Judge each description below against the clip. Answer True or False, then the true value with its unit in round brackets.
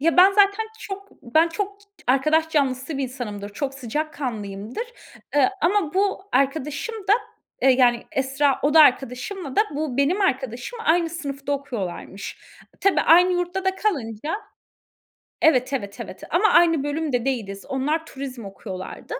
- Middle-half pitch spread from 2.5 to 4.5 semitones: False (5.3 semitones)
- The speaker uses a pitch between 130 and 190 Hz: False (280 Hz)